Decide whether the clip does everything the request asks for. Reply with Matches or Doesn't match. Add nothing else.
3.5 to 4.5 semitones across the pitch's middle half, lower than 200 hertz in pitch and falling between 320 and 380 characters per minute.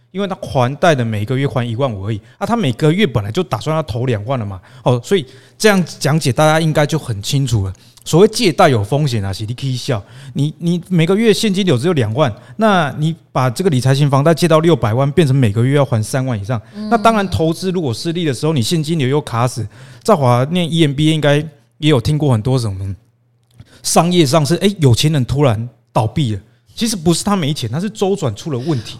Doesn't match